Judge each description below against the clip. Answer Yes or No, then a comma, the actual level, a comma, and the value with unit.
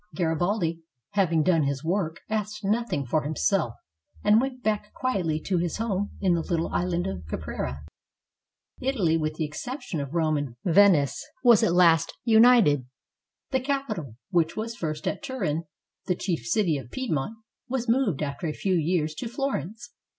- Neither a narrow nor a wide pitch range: No, wide, 6.0 semitones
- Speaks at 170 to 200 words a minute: No, average, 160 wpm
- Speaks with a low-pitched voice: No, medium, 175 Hz